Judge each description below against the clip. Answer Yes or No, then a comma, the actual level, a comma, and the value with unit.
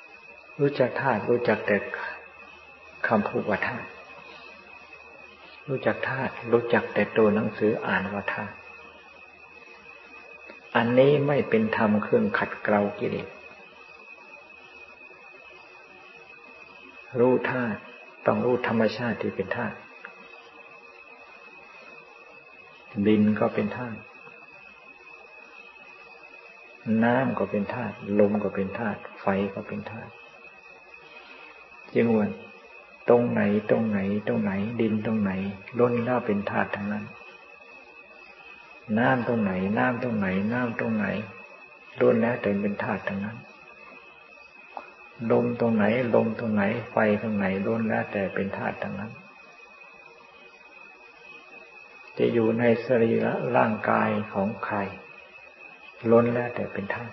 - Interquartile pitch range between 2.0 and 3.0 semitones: Yes, narrow, 2.6 semitones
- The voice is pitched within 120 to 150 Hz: No, low, 110 Hz